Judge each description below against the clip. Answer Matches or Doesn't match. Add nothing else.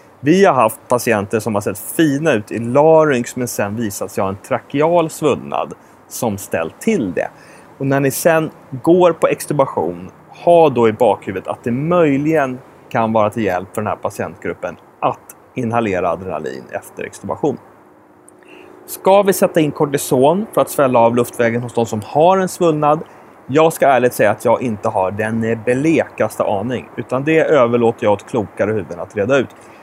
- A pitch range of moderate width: Doesn't match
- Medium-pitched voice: Doesn't match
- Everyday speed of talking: Matches